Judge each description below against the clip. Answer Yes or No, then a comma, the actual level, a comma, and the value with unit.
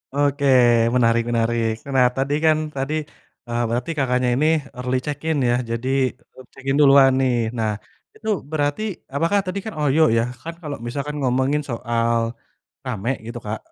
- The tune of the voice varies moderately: Yes, average, 3.6 semitones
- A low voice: Yes, low, 130 Hz